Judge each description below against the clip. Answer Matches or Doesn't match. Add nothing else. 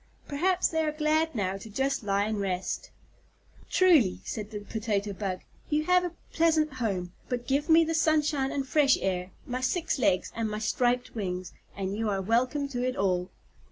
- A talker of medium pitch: Doesn't match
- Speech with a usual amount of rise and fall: Doesn't match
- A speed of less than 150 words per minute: Doesn't match